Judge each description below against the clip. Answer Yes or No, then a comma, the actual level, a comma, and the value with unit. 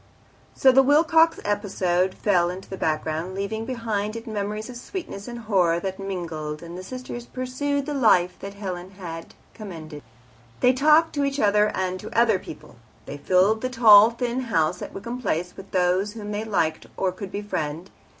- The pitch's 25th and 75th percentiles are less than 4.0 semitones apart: No, average, 4.8 semitones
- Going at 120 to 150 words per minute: No, average, 180 wpm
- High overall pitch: Yes, high, 205 Hz